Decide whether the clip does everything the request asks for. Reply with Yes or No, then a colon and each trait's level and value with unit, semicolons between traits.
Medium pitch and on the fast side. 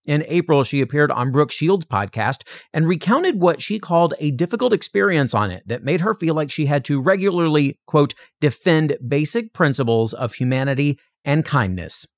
No: medium, 150 Hz; average, 170 wpm